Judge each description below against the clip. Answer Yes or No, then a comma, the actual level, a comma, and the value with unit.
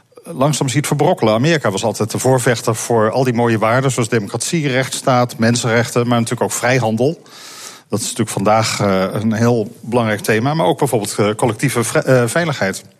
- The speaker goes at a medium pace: Yes, average, 155 wpm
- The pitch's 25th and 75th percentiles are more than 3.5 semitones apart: No, average, 3.1 semitones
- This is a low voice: Yes, low, 120 Hz